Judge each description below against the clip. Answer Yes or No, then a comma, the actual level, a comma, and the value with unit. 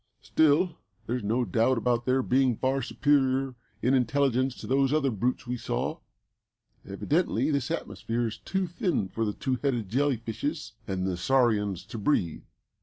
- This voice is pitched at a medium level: No, low, 130 Hz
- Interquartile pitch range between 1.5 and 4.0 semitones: Yes, average, 3.7 semitones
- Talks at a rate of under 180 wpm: Yes, average, 160 wpm